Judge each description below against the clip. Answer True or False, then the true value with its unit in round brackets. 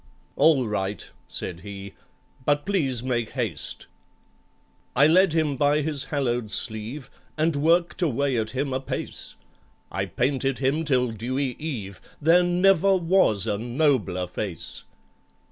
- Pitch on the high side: False (135 Hz)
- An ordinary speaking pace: False (130 wpm)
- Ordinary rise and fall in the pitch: False (5.8 semitones)